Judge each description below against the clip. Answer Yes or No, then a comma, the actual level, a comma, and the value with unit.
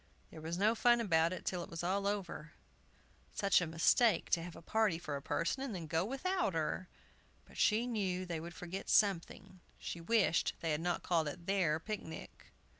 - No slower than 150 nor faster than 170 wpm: No, average, 195 wpm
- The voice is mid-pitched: Yes, medium, 180 Hz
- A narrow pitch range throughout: No, average, 3.9 semitones